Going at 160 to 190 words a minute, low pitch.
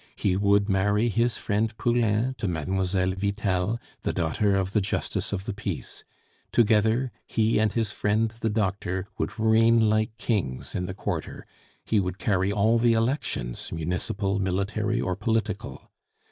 No: average, 150 wpm; low, 105 Hz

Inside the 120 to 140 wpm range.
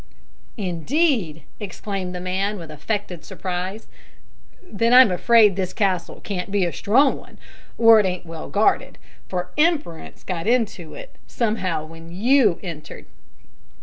Yes: slow, 135 wpm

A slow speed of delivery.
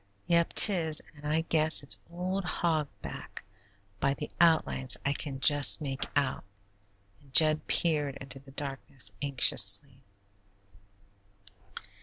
Yes: slow, 120 wpm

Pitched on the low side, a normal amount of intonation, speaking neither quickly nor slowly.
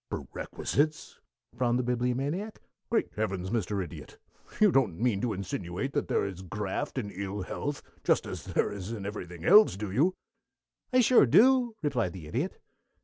No: low, 115 Hz; wide, 7.1 semitones; average, 160 wpm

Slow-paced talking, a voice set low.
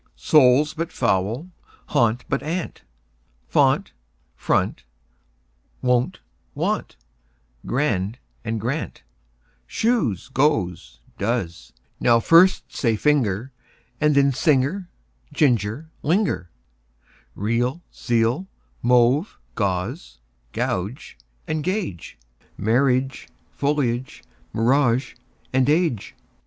Yes: slow, 80 wpm; low, 125 Hz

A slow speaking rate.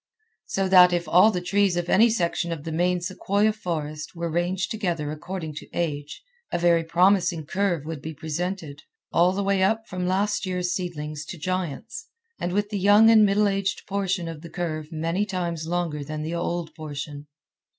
No: average, 185 wpm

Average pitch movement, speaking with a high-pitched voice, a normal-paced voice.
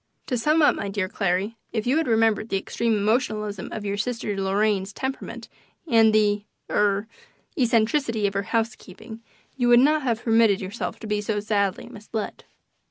No: narrow, 2.3 semitones; high, 215 Hz; average, 165 wpm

